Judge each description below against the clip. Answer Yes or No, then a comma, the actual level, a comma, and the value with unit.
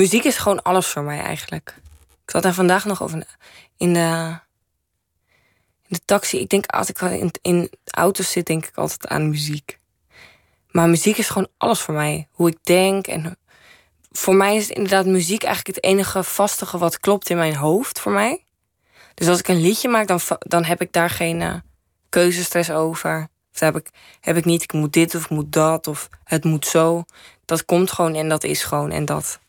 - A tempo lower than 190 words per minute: No, fast, 200 wpm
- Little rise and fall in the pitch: No, average, 3.2 semitones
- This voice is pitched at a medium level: Yes, medium, 170 Hz